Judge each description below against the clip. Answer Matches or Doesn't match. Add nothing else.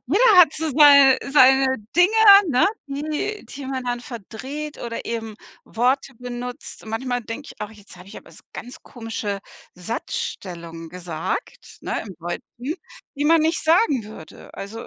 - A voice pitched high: Matches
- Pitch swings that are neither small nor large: Matches